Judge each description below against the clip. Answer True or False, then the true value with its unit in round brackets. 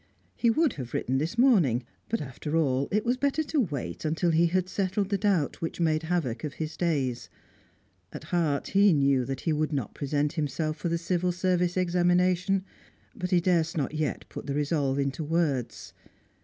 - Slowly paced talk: False (185 wpm)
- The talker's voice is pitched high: False (165 Hz)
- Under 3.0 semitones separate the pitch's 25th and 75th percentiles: False (4.2 semitones)